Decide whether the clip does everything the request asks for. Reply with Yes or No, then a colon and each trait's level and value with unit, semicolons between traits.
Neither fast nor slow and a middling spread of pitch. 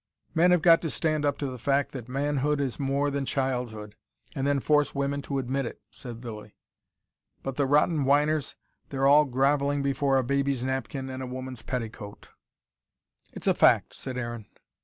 No: average, 180 wpm; narrow, 1.9 semitones